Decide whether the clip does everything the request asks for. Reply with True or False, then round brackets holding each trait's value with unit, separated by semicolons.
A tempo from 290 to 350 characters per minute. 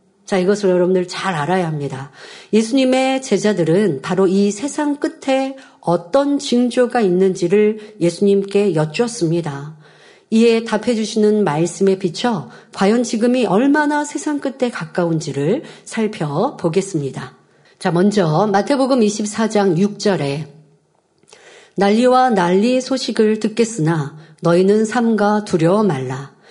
False (265 characters per minute)